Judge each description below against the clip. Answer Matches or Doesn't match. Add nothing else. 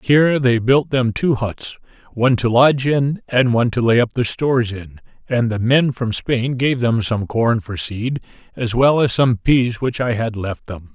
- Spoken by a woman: Doesn't match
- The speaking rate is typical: Doesn't match